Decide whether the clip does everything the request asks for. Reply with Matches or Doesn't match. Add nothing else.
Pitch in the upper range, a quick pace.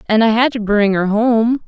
Matches